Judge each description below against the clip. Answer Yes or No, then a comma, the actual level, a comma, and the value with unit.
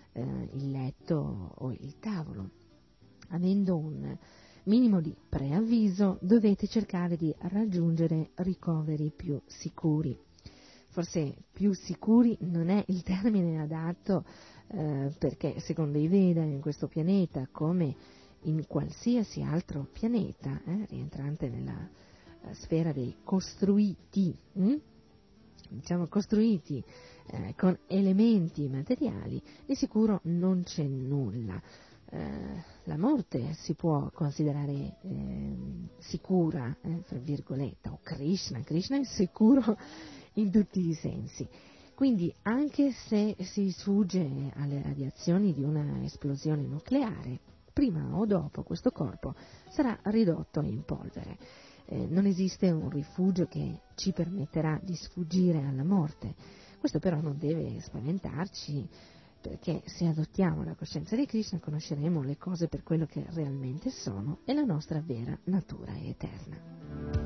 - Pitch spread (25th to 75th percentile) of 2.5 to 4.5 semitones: No, average, 4.9 semitones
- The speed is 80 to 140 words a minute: Yes, average, 120 wpm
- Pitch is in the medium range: Yes, medium, 165 Hz